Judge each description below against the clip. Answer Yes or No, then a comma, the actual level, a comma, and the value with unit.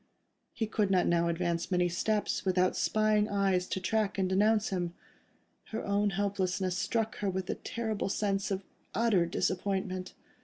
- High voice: Yes, high, 195 Hz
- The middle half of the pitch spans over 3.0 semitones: No, narrow, 2.4 semitones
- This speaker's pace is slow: No, average, 155 wpm